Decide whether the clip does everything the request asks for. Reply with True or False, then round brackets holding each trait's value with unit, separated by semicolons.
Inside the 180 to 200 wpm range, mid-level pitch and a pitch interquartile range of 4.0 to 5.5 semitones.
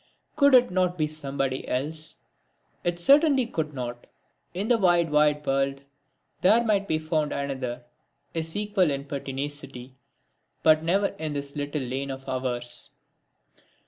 False (140 wpm; 150 Hz; 4.7 semitones)